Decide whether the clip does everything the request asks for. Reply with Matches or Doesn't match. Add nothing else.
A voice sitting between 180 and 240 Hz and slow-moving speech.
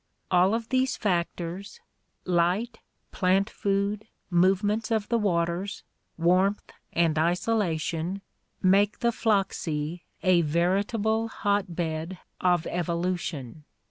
Matches